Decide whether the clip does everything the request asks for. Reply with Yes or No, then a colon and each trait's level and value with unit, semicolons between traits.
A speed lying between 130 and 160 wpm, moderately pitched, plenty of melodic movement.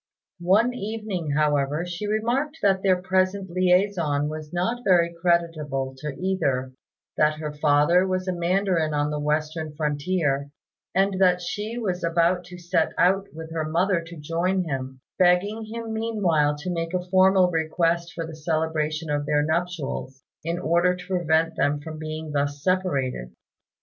No: average, 155 wpm; medium, 170 Hz; average, 3.5 semitones